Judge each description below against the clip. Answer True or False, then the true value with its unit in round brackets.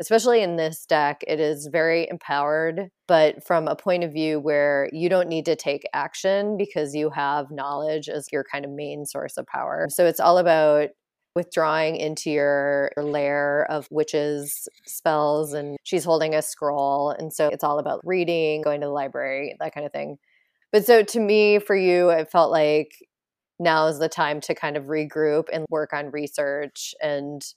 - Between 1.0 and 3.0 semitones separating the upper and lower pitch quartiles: True (2.4 semitones)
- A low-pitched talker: False (155 Hz)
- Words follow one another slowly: False (185 wpm)